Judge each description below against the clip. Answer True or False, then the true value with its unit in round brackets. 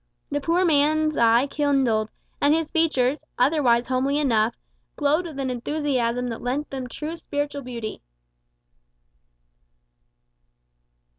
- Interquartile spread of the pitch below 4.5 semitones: True (3.4 semitones)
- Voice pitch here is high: True (280 Hz)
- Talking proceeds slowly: True (115 wpm)